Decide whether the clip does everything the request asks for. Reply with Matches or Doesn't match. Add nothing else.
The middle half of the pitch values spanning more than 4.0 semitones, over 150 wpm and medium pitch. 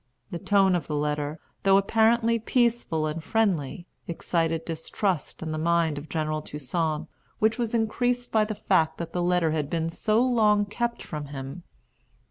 Matches